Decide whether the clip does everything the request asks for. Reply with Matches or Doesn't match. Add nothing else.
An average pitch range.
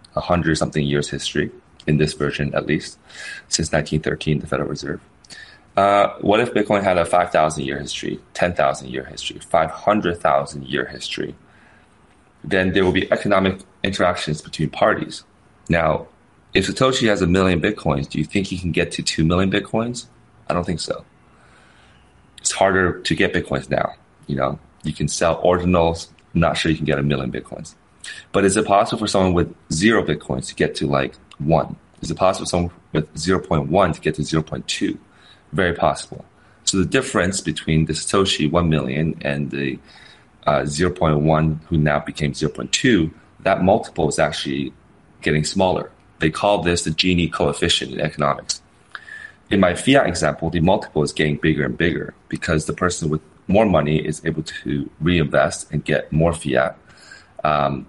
Matches